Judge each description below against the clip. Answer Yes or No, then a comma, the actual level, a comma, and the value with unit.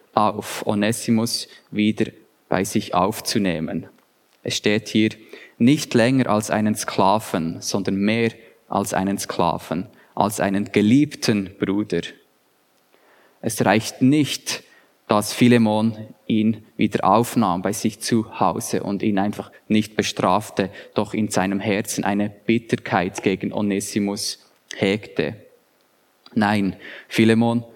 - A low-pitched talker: Yes, low, 110 Hz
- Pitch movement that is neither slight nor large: No, narrow, 2.2 semitones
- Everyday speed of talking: No, slow, 110 wpm